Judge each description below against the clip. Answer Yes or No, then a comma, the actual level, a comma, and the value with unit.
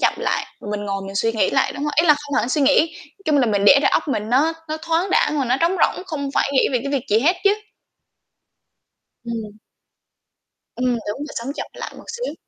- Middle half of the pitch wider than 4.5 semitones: Yes, average, 4.9 semitones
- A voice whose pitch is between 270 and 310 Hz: Yes, very high, 280 Hz